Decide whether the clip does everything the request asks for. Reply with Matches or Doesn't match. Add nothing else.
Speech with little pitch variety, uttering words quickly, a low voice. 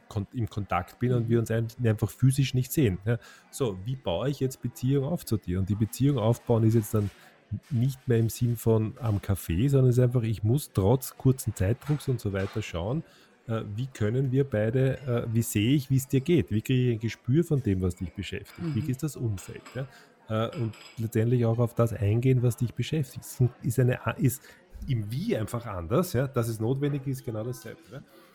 Doesn't match